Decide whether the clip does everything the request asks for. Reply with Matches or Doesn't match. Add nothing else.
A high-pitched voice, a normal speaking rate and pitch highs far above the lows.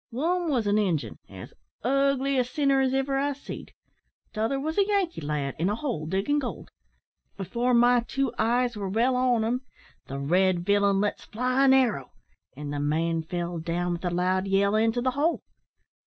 Matches